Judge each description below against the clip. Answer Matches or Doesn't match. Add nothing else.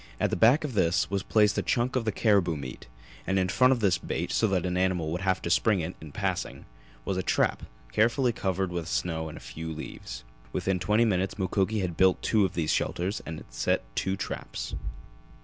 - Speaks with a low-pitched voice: Matches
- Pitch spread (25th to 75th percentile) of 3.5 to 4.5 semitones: Matches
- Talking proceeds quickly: Matches